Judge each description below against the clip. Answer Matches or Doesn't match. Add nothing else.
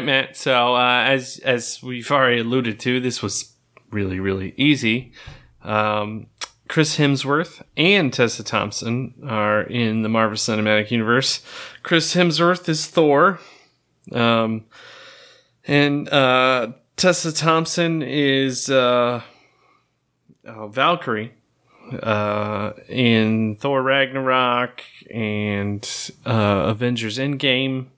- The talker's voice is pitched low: Matches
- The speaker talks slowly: Matches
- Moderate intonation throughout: Matches